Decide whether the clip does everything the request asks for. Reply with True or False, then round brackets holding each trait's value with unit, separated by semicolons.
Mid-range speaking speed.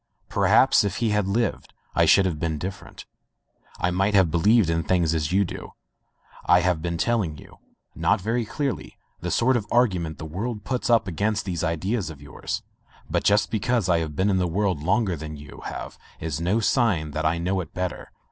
False (210 wpm)